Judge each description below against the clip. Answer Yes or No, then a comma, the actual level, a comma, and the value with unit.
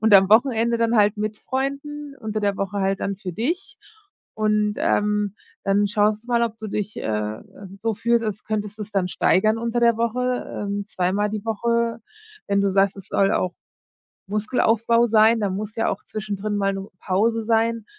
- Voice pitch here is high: Yes, high, 215 Hz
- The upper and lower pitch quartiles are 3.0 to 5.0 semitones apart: No, narrow, 2.4 semitones